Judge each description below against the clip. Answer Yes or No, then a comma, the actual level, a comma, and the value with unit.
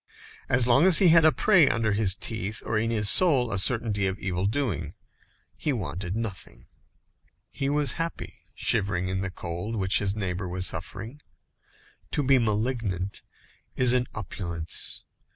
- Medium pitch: No, low, 110 Hz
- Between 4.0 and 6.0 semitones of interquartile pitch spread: Yes, average, 5.1 semitones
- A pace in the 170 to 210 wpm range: No, average, 155 wpm